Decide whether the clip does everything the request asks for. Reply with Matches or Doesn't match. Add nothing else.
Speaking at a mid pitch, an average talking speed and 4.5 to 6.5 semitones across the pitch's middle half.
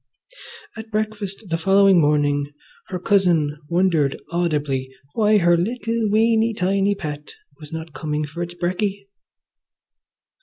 Doesn't match